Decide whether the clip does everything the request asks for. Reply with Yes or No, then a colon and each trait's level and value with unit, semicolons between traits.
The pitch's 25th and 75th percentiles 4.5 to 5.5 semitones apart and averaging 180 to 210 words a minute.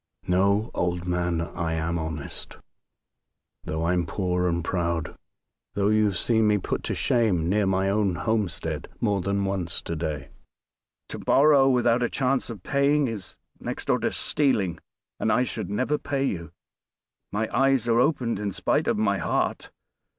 No: average, 5.1 semitones; average, 165 wpm